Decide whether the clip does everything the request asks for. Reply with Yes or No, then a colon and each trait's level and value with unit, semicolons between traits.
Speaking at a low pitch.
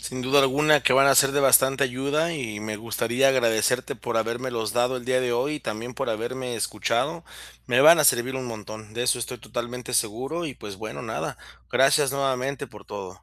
Yes: low, 125 Hz